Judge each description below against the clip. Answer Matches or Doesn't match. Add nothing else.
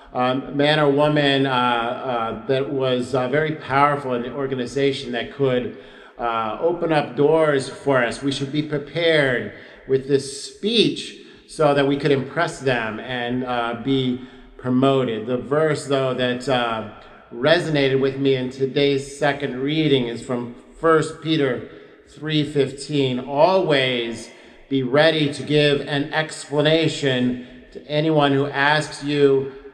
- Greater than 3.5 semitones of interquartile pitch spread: Doesn't match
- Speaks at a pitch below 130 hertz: Doesn't match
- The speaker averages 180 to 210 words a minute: Doesn't match